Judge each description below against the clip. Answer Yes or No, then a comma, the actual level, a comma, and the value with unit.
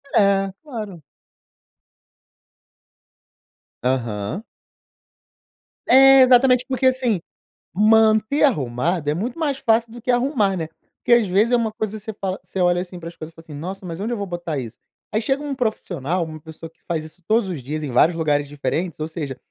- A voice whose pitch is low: No, high, 190 Hz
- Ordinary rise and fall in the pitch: No, wide, 6.7 semitones